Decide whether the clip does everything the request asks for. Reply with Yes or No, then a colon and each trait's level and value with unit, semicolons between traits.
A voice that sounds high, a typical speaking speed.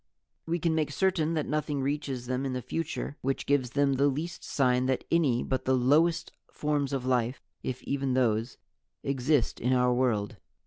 No: low, 135 Hz; average, 180 wpm